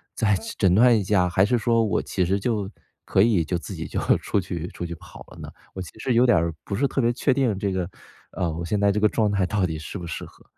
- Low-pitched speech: Yes, low, 100 Hz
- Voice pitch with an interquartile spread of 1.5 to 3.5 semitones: No, average, 3.9 semitones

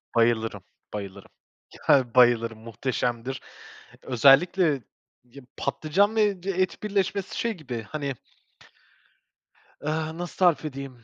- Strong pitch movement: Yes, wide, 6.9 semitones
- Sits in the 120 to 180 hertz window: Yes, medium, 140 Hz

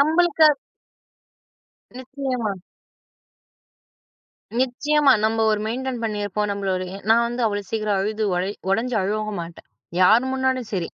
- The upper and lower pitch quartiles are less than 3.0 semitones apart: No, average, 4.2 semitones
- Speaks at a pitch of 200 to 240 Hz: Yes, high, 220 Hz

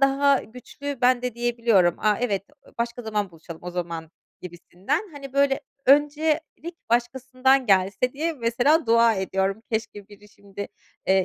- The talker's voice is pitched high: Yes, high, 235 Hz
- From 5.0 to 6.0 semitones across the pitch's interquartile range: Yes, wide, 5.6 semitones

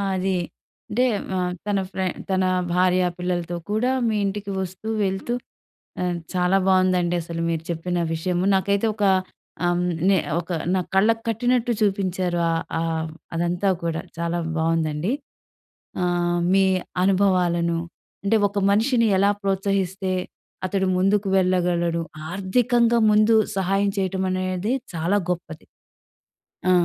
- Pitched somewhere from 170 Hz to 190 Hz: Yes, medium, 185 Hz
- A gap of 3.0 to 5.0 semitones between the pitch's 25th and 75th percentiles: No, narrow, 2.4 semitones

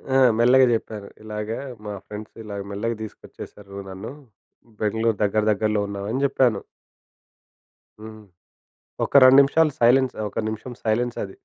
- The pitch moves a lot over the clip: No, average, 2.9 semitones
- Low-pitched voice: Yes, low, 110 Hz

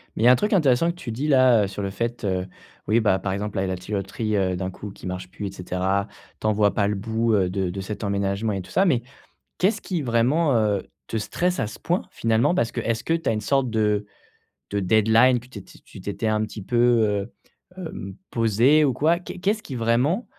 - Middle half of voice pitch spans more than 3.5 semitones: Yes, average, 4.3 semitones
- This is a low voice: Yes, low, 110 Hz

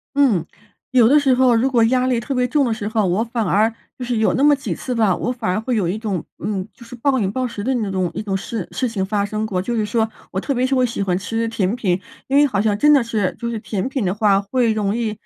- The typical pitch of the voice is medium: No, high, 225 Hz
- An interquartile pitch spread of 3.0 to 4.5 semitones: Yes, average, 3.7 semitones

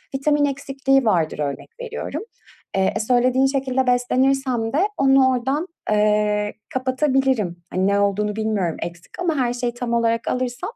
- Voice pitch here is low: No, high, 245 Hz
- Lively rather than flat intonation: No, average, 4.3 semitones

